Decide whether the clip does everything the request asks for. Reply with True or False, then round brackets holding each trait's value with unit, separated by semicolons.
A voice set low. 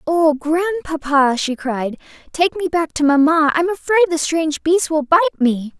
False (320 Hz)